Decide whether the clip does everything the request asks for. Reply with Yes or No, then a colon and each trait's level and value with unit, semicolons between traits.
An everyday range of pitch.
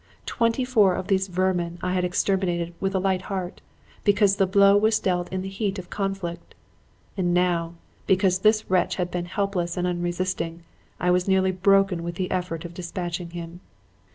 No: narrow, 1.8 semitones